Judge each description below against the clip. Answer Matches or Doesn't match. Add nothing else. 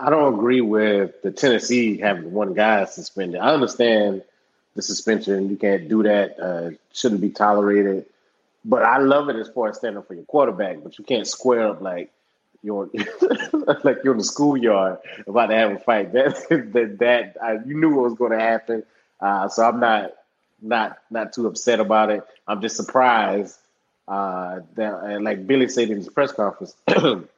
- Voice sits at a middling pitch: Doesn't match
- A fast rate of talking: Doesn't match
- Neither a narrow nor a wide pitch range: Matches